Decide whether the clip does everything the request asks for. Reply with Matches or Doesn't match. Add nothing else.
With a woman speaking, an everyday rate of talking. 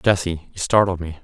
Doesn't match